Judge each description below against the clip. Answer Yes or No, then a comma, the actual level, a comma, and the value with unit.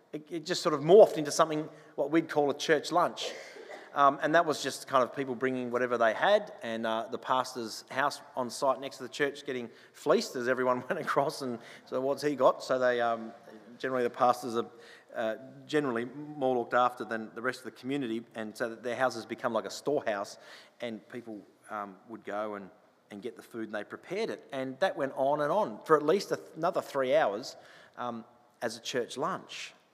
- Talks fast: Yes, fast, 210 wpm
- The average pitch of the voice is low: Yes, low, 130 Hz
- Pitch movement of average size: Yes, average, 3.6 semitones